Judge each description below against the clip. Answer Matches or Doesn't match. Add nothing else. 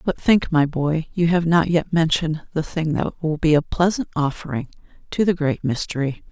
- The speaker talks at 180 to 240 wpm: Matches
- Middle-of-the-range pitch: Matches